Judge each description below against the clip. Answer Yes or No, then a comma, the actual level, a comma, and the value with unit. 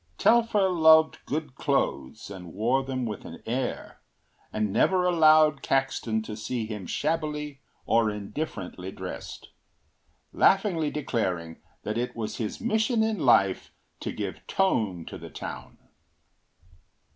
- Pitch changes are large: Yes, wide, 6.9 semitones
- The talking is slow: Yes, slow, 125 wpm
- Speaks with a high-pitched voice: No, low, 130 Hz